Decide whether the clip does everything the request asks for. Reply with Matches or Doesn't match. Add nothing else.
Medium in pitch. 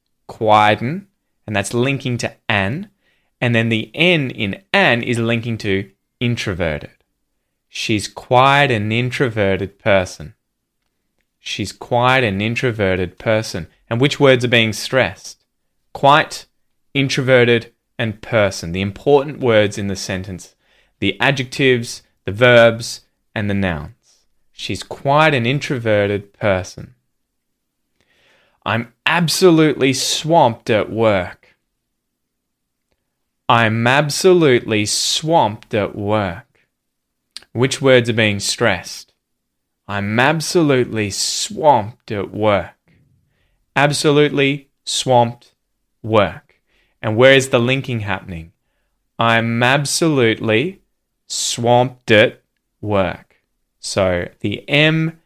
Doesn't match